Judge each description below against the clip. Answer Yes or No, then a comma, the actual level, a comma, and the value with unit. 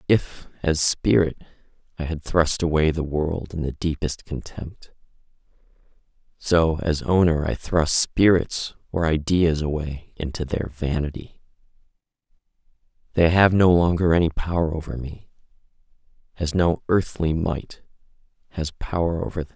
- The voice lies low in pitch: Yes, very low, 80 Hz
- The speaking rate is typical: No, slow, 130 wpm